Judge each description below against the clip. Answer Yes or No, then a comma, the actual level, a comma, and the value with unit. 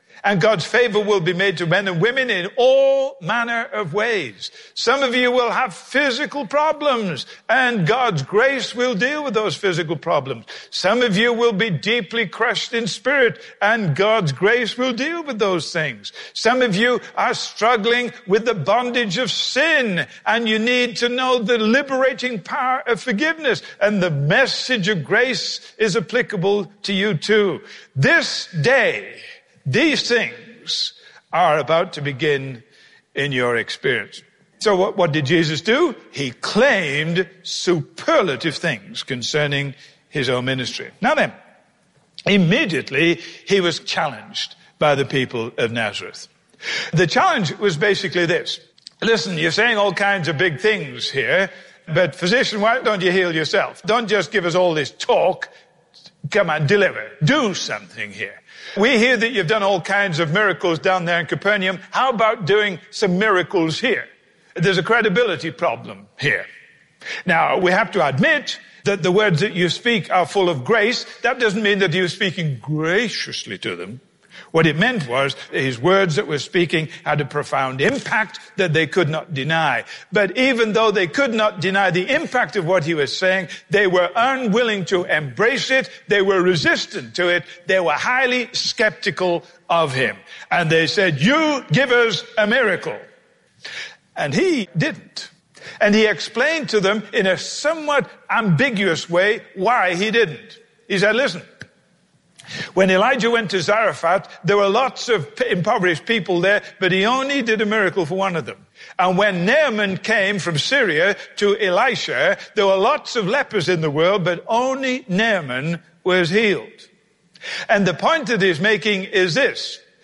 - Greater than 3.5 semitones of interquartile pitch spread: Yes, average, 5.2 semitones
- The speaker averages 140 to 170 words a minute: Yes, average, 160 wpm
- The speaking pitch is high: Yes, high, 200 Hz